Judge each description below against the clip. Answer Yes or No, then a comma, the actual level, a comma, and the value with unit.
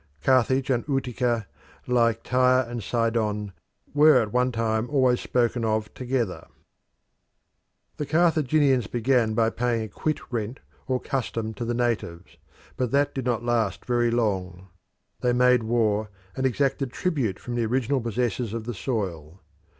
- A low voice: Yes, low, 120 Hz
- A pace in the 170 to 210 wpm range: No, average, 145 wpm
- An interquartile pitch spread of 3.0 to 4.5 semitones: No, narrow, 2.6 semitones